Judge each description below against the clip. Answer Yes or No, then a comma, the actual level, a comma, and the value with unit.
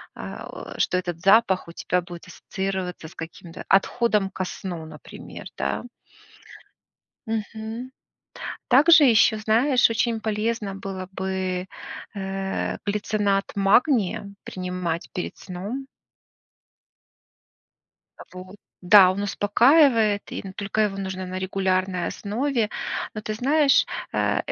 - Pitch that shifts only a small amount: No, average, 3.1 semitones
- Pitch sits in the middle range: No, high, 195 Hz